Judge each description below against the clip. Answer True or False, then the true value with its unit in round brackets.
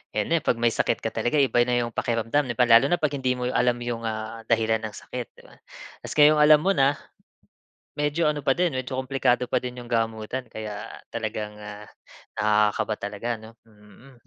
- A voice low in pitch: True (120 Hz)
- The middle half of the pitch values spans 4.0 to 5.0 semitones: False (3.5 semitones)